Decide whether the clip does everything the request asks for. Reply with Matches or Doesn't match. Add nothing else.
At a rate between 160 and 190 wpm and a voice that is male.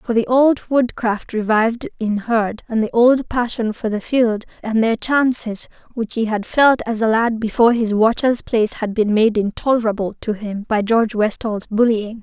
Doesn't match